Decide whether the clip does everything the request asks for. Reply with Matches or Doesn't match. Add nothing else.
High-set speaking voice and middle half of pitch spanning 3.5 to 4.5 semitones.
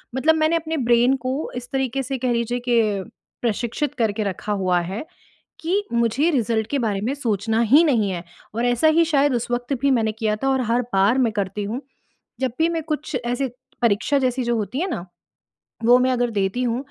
Matches